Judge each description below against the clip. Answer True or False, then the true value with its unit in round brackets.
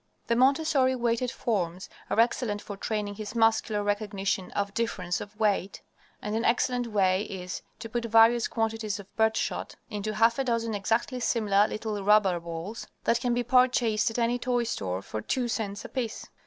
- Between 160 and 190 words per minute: True (170 wpm)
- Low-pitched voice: False (220 Hz)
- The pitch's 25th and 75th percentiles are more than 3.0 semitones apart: False (2.6 semitones)